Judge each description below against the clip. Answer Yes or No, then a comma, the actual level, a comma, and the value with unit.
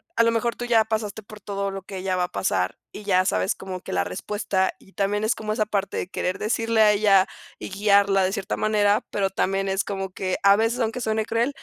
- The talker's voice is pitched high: Yes, high, 200 Hz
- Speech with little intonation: Yes, narrow, 2.2 semitones